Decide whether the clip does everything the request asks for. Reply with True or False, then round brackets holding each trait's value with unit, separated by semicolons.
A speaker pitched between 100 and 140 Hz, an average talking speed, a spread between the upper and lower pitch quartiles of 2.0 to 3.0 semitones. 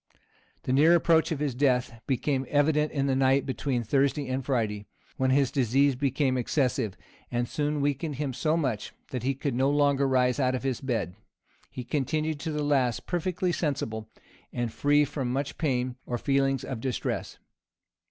True (135 Hz; 170 wpm; 2.5 semitones)